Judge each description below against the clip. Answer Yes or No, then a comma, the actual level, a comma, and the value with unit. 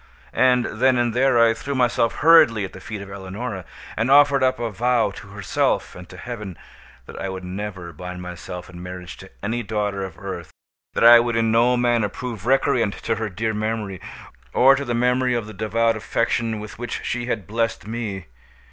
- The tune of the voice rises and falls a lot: No, average, 3.7 semitones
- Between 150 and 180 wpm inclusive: No, average, 195 wpm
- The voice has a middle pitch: No, low, 110 Hz